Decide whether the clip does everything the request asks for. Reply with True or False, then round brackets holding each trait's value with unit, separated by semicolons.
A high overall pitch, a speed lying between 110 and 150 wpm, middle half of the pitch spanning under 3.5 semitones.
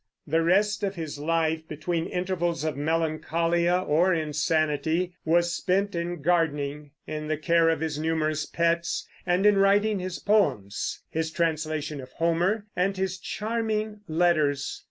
False (165 Hz; 140 wpm; 2.8 semitones)